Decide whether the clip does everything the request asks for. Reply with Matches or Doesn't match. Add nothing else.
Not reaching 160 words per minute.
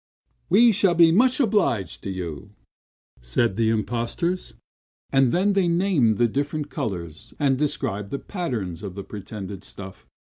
Matches